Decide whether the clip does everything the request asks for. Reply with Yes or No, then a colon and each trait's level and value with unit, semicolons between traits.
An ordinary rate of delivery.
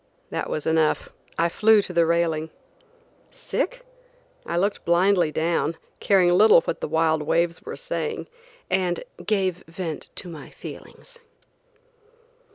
No: slow, 130 wpm